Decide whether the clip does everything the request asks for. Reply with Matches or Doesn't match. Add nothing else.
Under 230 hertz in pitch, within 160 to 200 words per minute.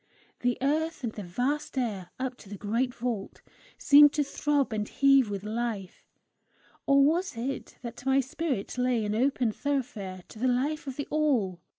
Doesn't match